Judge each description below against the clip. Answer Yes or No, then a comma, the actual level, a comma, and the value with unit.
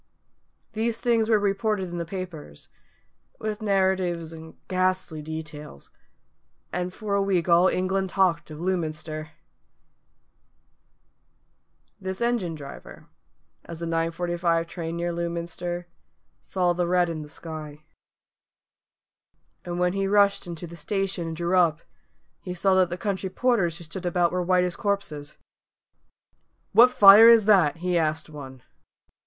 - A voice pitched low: No, medium, 175 Hz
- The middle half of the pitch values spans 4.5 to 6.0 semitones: No, average, 2.7 semitones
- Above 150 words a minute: No, slow, 135 wpm